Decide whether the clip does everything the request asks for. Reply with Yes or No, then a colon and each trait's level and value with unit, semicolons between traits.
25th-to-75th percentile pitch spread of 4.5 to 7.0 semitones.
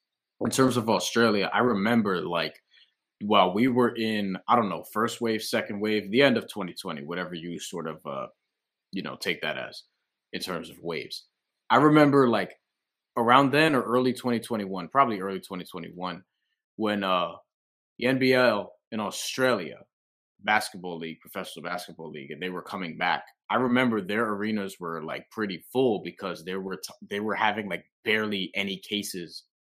No: average, 4.1 semitones